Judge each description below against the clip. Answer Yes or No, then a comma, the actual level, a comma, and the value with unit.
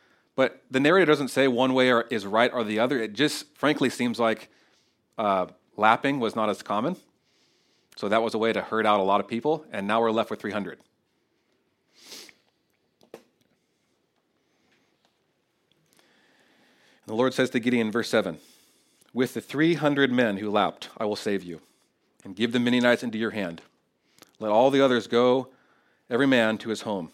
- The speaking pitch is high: No, low, 120 Hz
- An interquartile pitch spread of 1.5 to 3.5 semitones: Yes, average, 3.0 semitones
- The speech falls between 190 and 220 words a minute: No, average, 170 wpm